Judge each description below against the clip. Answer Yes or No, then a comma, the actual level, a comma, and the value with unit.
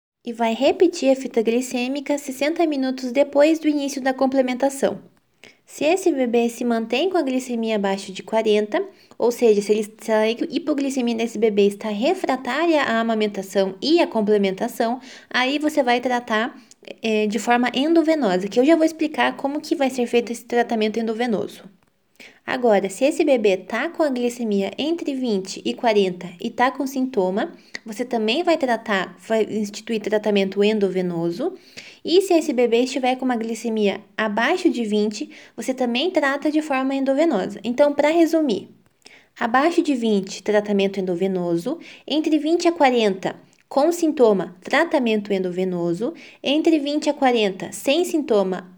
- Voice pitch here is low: No, high, 245 Hz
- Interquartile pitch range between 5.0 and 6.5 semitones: Yes, average, 5.3 semitones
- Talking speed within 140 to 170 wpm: Yes, average, 150 wpm